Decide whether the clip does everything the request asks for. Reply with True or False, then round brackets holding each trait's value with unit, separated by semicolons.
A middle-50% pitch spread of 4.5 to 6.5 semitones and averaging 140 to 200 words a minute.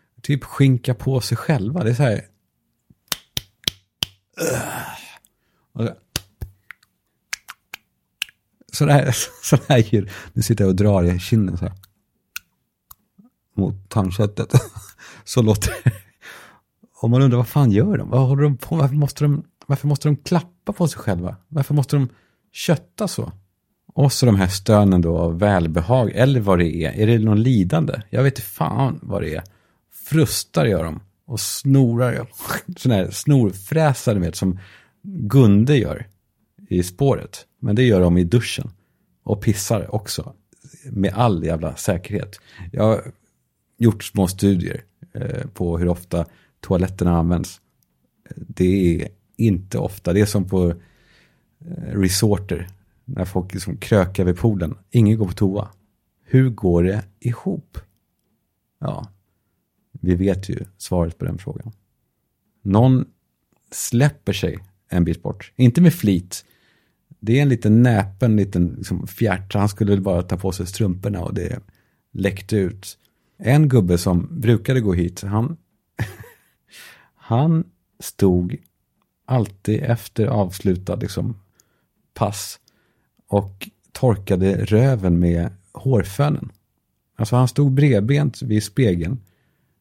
False (5.2 semitones; 130 wpm)